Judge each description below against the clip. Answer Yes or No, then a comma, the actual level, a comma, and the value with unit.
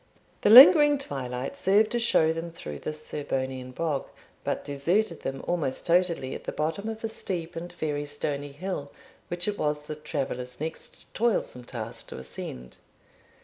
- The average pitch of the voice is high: No, medium, 155 Hz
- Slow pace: No, average, 160 wpm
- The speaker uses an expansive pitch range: No, average, 5.0 semitones